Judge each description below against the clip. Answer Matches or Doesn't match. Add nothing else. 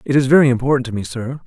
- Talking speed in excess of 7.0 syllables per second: Matches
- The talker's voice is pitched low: Matches